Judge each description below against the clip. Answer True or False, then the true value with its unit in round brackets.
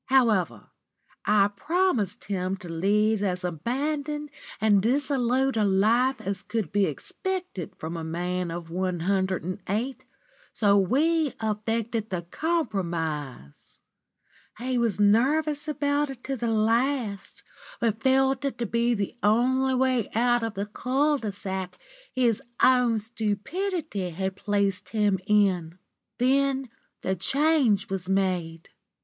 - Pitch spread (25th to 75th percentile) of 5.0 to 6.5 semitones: True (5.5 semitones)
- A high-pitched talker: True (215 Hz)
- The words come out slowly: True (130 wpm)